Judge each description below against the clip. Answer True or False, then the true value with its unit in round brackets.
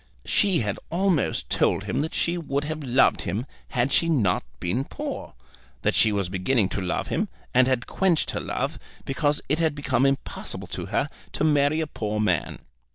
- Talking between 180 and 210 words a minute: True (185 wpm)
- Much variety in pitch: True (6.4 semitones)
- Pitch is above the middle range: False (135 Hz)